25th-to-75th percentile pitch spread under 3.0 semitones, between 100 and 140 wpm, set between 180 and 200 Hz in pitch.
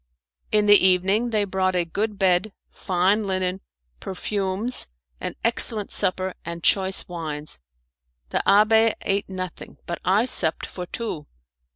Yes: narrow, 2.5 semitones; slow, 135 wpm; high, 190 Hz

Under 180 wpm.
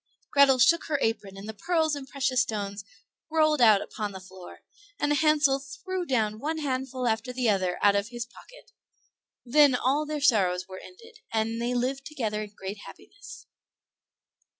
Yes: average, 170 wpm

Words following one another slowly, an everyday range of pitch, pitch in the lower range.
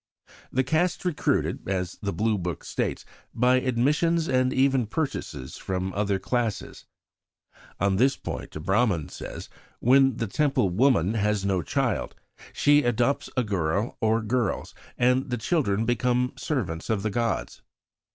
No: average, 145 wpm; average, 4.8 semitones; low, 115 Hz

